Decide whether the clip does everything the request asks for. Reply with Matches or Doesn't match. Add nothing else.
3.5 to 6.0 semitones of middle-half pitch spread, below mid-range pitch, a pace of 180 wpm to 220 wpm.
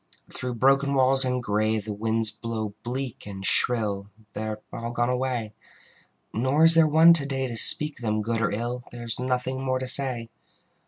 Doesn't match